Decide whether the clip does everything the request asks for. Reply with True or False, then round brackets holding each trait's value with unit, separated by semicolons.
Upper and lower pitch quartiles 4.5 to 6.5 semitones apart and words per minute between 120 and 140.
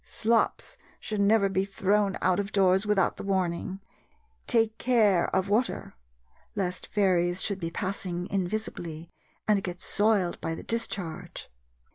False (2.7 semitones; 135 wpm)